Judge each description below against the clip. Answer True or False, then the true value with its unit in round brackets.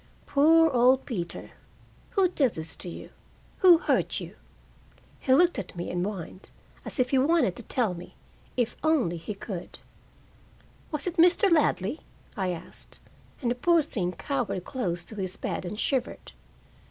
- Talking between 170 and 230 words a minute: False (160 wpm)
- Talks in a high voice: True (245 Hz)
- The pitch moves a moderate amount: False (8.9 semitones)